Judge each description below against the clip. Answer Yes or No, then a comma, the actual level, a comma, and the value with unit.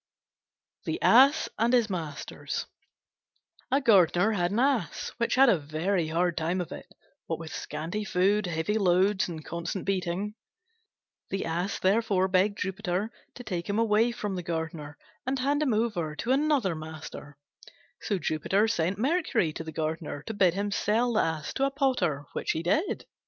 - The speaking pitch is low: No, high, 190 Hz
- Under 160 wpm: No, average, 170 wpm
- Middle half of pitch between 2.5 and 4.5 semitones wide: No, average, 5.2 semitones